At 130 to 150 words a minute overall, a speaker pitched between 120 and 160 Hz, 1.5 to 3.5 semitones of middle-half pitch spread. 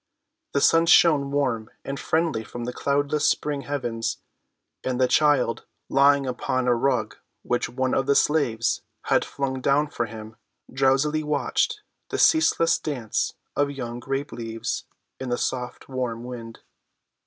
Yes: average, 145 wpm; low, 135 Hz; average, 3.0 semitones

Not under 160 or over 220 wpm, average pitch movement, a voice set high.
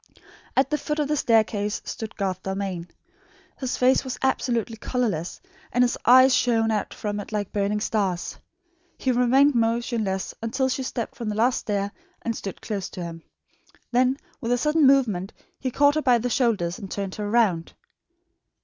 Yes: average, 175 wpm; average, 4.1 semitones; high, 230 Hz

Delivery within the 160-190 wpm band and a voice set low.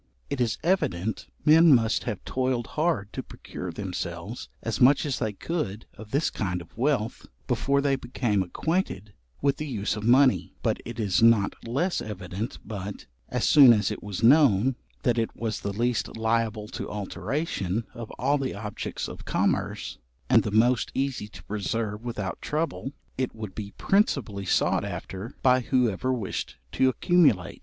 Yes: average, 165 wpm; low, 115 Hz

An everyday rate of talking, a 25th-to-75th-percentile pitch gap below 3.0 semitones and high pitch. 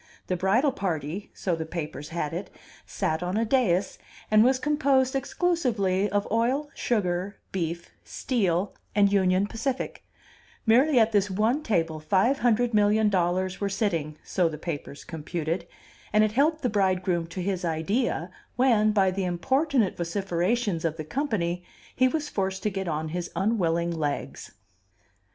No: average, 150 wpm; average, 5.1 semitones; high, 195 Hz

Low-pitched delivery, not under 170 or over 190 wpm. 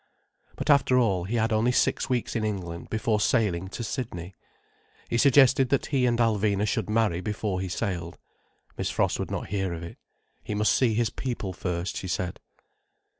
Yes: low, 105 Hz; average, 180 wpm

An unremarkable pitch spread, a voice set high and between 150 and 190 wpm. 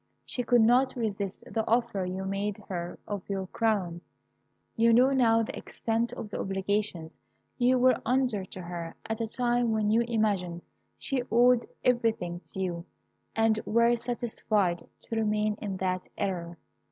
Yes: average, 3.8 semitones; high, 215 Hz; average, 155 wpm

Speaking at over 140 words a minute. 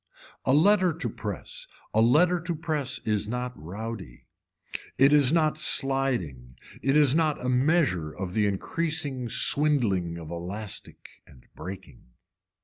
No: slow, 135 wpm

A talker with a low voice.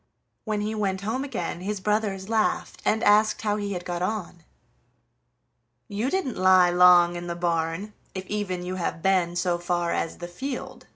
No: medium, 185 Hz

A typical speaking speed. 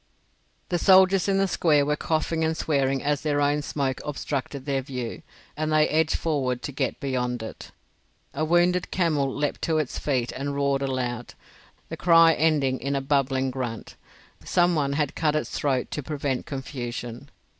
Yes: average, 170 wpm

